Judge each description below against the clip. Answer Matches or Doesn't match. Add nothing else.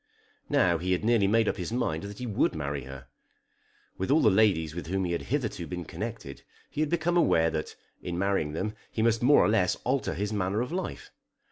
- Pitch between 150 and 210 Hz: Doesn't match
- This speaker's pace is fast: Matches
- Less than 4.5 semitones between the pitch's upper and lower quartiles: Doesn't match